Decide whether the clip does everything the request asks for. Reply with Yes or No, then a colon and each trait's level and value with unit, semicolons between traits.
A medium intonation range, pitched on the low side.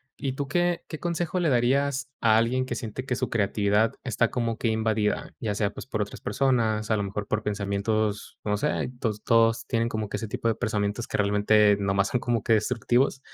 Yes: average, 3.3 semitones; low, 110 Hz